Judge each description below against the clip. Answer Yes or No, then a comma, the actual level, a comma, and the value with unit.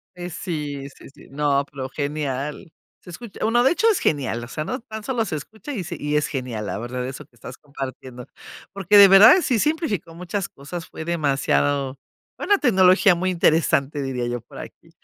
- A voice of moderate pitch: Yes, medium, 155 Hz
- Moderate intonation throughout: No, wide, 6.1 semitones